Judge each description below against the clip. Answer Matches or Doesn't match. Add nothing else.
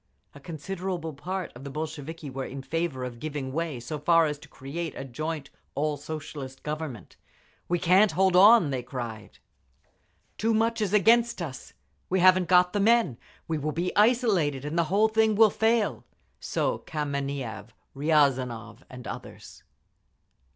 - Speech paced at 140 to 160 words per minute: Matches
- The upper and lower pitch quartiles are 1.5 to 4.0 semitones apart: Doesn't match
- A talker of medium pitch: Matches